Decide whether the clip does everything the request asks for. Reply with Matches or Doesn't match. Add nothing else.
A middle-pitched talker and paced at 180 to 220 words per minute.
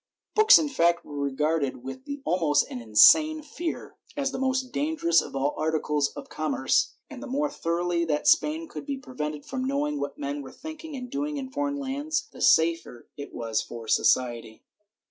Matches